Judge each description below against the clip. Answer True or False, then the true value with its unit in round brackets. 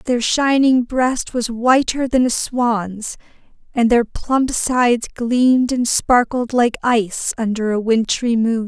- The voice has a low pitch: False (240 Hz)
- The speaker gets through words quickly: False (145 wpm)